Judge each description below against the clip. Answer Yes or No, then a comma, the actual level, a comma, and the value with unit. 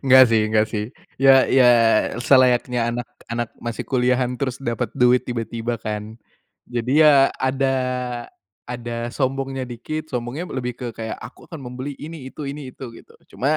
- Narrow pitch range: Yes, narrow, 2.2 semitones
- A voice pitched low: Yes, low, 125 Hz